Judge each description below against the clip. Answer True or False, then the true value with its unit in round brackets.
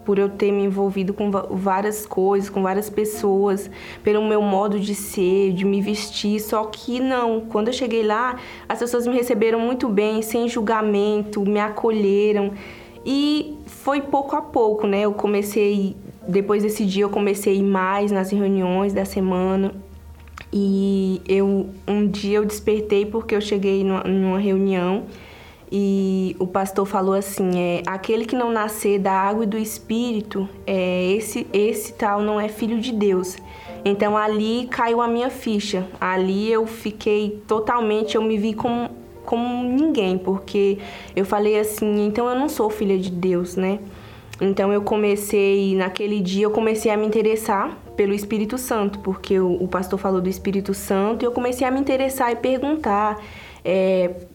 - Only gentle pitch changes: True (2.1 semitones)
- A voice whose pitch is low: False (205 Hz)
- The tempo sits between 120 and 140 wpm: False (165 wpm)